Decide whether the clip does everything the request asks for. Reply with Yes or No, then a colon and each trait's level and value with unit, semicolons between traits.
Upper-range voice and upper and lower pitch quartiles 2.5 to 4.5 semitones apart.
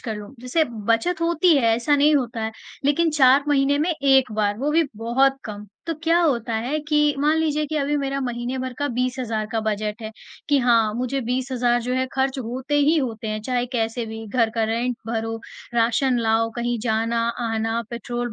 Yes: high, 245 Hz; average, 3.6 semitones